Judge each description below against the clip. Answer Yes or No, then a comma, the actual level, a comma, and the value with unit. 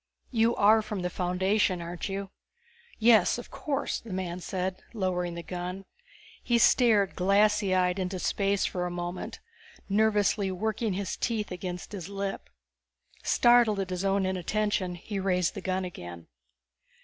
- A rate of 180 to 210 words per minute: No, average, 150 wpm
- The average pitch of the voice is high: Yes, high, 195 Hz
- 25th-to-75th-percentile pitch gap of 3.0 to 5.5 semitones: No, narrow, 2.6 semitones